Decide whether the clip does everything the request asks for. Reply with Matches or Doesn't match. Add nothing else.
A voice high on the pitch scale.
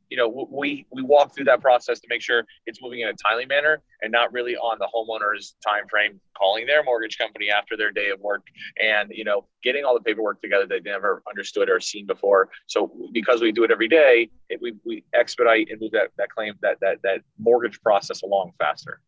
Doesn't match